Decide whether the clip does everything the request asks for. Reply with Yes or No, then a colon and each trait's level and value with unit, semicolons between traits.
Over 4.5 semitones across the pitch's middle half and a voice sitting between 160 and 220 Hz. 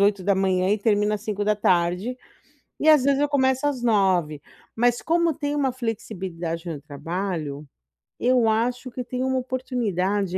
Yes: wide, 5.6 semitones; high, 215 Hz